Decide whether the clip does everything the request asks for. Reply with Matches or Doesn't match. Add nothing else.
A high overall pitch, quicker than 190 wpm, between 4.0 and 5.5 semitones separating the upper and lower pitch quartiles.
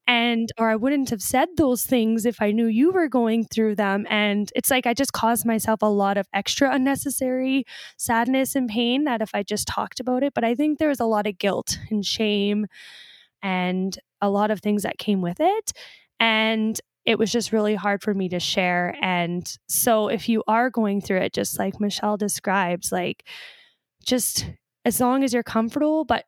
Doesn't match